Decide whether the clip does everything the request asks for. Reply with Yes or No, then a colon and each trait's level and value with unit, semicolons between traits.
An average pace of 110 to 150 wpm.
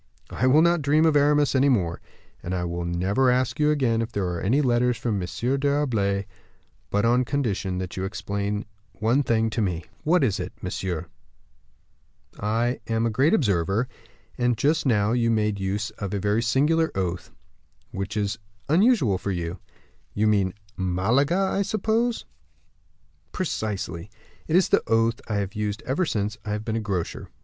No: average, 175 wpm